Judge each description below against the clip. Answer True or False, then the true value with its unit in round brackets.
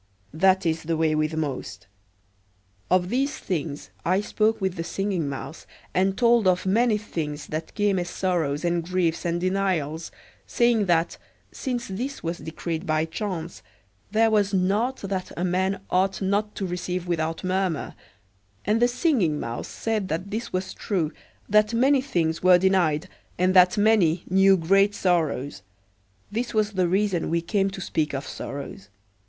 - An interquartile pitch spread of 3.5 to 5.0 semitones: True (3.9 semitones)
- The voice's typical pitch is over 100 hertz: True (185 Hz)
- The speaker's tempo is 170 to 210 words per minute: False (160 wpm)